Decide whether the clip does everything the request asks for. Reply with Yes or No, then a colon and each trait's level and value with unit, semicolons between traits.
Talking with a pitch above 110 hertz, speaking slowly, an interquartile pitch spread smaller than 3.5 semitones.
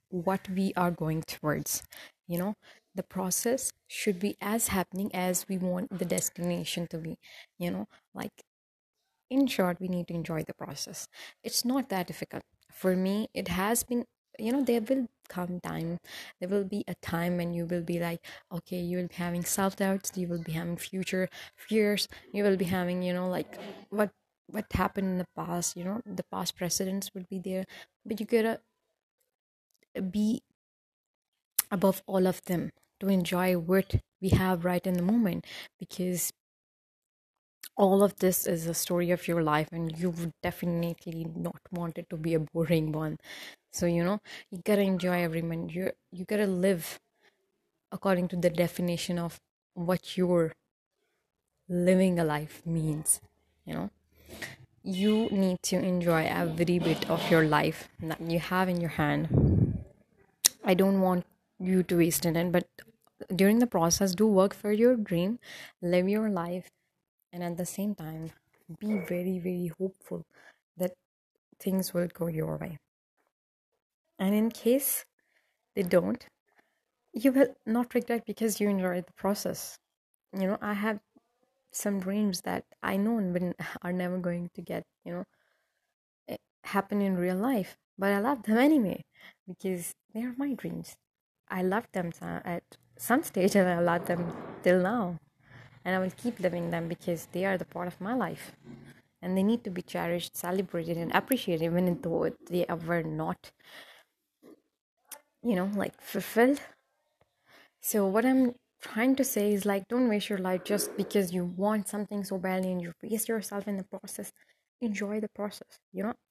No: medium, 185 Hz; average, 165 wpm; average, 2.9 semitones